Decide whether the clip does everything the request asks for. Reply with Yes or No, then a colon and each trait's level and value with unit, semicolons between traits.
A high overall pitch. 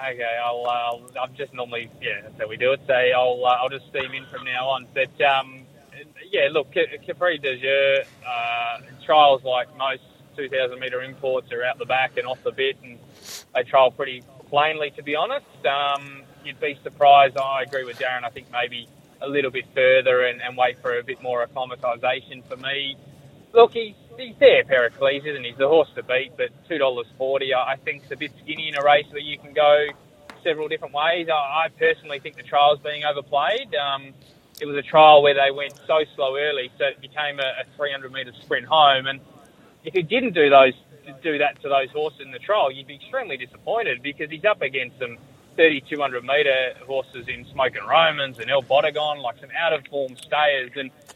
No: medium, 140 Hz